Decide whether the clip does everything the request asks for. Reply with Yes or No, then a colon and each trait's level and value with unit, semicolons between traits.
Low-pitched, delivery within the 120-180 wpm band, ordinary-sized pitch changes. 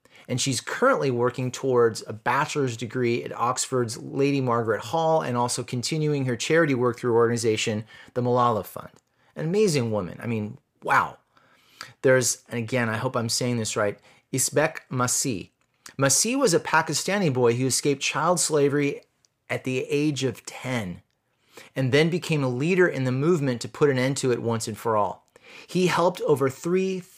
Yes: low, 130 Hz; average, 170 wpm; average, 3.5 semitones